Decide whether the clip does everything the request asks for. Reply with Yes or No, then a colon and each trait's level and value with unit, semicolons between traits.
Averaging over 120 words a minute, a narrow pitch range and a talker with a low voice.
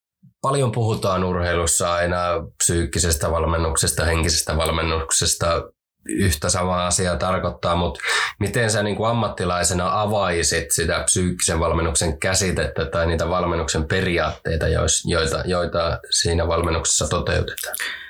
No: average, 105 wpm; narrow, 2.0 semitones; very low, 85 Hz